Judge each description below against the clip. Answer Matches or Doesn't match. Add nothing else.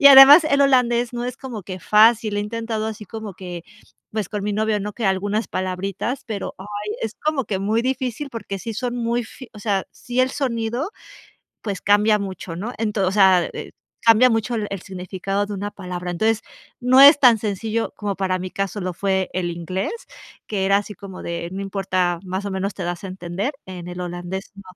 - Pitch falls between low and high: Doesn't match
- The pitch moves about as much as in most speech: Matches